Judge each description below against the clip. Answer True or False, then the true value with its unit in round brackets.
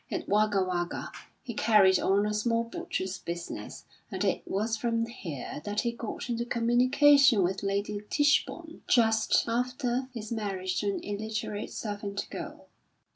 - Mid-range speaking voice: False (215 Hz)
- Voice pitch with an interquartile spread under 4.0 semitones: True (3.0 semitones)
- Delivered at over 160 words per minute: False (145 wpm)